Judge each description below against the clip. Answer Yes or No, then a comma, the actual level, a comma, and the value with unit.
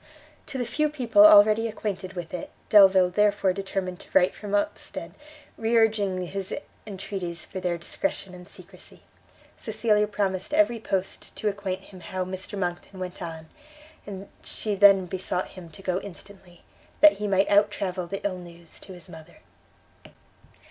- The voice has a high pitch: Yes, high, 195 Hz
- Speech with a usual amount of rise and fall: No, narrow, 2.3 semitones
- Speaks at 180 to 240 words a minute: No, average, 160 wpm